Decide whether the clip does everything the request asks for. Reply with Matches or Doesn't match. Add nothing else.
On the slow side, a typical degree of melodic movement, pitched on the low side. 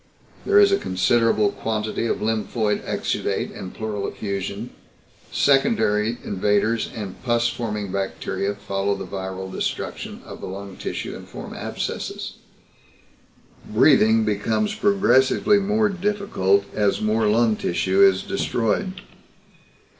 Matches